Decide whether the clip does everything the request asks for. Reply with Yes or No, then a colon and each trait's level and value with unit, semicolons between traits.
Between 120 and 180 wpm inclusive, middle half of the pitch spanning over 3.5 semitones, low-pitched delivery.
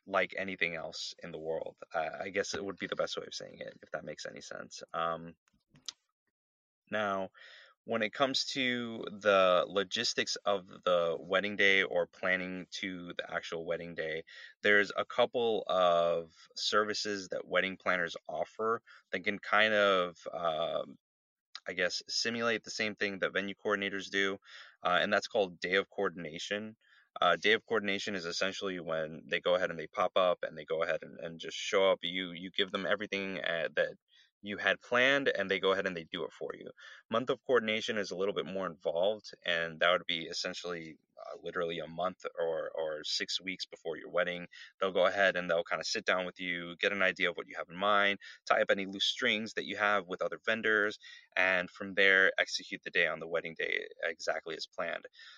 No: average, 200 wpm; average, 4.1 semitones; low, 100 Hz